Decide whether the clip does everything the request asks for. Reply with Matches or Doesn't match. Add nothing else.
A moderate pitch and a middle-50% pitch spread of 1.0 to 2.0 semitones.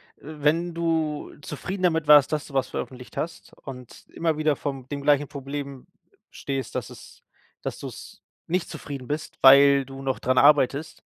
Doesn't match